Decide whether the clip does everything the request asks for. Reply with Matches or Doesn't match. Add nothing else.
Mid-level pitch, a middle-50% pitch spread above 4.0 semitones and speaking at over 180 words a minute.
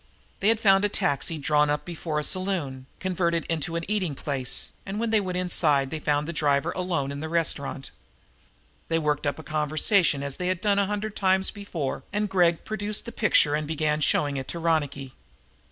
Matches